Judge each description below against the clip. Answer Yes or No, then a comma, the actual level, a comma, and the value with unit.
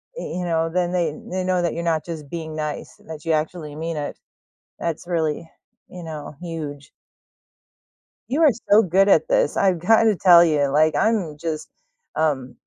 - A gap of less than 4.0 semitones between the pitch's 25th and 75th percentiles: Yes, average, 3.0 semitones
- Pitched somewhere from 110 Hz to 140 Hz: No, medium, 165 Hz